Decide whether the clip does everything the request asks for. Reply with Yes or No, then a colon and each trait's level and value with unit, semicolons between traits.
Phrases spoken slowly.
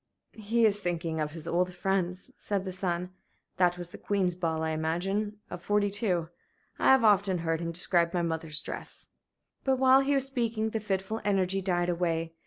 No: average, 185 wpm